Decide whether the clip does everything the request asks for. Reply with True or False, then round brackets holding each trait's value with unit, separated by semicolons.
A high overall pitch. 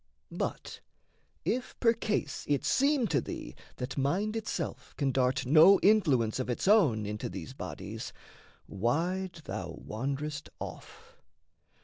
False (150 Hz)